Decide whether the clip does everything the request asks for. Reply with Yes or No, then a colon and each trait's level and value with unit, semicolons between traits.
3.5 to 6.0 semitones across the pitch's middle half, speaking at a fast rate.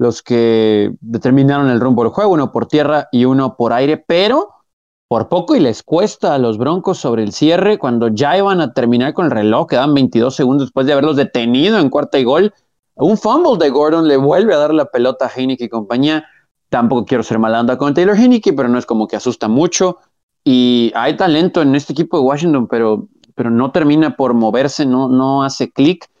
Yes: average, 4.2 semitones; fast, 210 wpm